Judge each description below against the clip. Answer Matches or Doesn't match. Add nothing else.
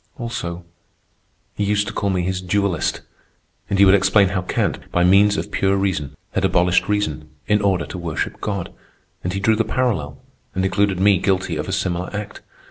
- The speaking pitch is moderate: Doesn't match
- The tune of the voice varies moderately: Doesn't match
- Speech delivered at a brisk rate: Doesn't match